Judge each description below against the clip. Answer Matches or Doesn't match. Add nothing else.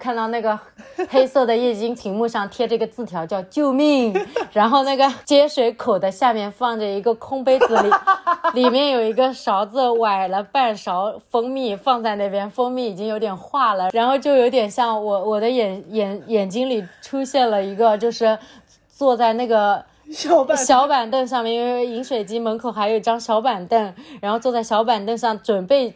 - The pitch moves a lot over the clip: Doesn't match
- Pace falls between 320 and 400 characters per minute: Doesn't match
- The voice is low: Doesn't match